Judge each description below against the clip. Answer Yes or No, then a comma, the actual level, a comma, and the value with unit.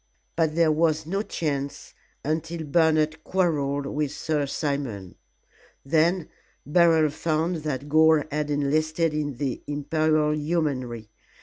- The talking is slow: Yes, slow, 115 wpm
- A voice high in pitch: No, medium, 155 Hz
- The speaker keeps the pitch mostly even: Yes, narrow, 1.9 semitones